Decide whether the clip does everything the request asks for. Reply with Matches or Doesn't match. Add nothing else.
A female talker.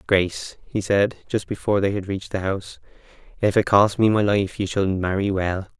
Doesn't match